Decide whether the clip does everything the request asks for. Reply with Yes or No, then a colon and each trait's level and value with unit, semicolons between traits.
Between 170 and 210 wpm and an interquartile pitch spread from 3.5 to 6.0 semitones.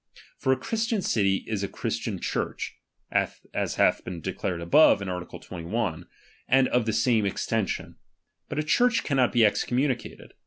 No: average, 155 wpm; wide, 5.5 semitones